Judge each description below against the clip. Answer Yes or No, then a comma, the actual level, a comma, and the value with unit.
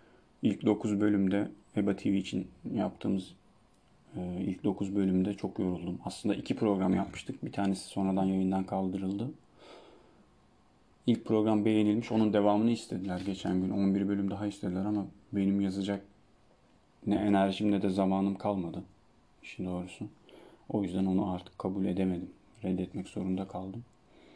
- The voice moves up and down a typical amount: No, narrow, 1.6 semitones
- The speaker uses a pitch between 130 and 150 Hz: No, low, 100 Hz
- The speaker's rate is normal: Yes, average, 130 wpm